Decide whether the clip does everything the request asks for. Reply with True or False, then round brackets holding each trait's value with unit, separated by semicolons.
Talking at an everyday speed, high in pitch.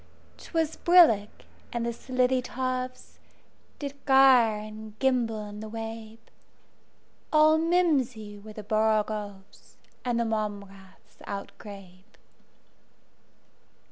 False (90 wpm; 225 Hz)